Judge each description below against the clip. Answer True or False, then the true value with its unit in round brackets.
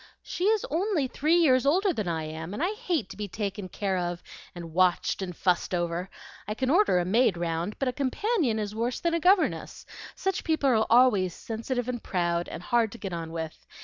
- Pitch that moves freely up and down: True (8.5 semitones)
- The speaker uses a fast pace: True (215 wpm)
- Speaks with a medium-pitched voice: False (220 Hz)